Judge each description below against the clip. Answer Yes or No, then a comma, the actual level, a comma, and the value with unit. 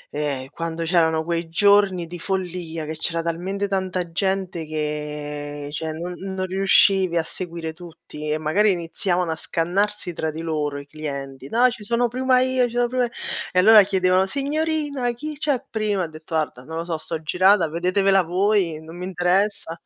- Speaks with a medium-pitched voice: Yes, medium, 175 Hz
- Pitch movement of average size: Yes, average, 4.0 semitones